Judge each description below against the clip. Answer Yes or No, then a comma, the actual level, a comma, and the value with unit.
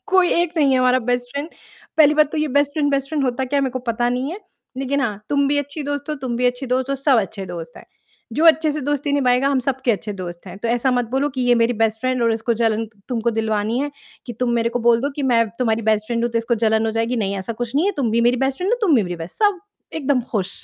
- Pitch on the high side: Yes, very high, 250 Hz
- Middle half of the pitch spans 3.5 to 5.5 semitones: Yes, average, 3.8 semitones